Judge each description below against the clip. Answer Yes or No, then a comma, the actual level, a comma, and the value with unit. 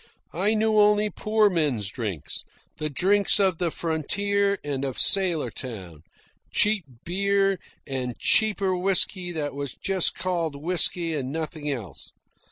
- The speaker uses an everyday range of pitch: No, wide, 5.8 semitones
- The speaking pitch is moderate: Yes, medium, 175 Hz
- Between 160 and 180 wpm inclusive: No, slow, 135 wpm